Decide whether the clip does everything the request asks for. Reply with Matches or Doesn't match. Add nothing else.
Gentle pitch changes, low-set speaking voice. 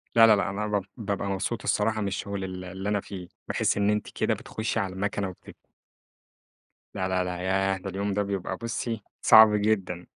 Matches